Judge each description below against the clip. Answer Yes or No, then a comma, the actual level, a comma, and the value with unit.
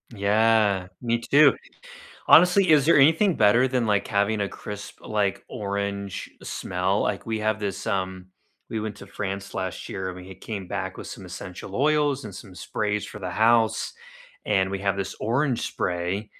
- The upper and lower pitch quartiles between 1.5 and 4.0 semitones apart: Yes, average, 2.9 semitones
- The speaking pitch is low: Yes, low, 105 Hz